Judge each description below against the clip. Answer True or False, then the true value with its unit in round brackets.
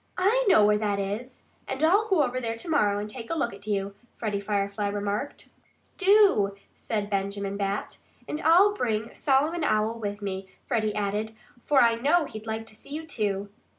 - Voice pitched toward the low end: False (220 Hz)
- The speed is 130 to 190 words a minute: True (185 wpm)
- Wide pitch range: True (5.9 semitones)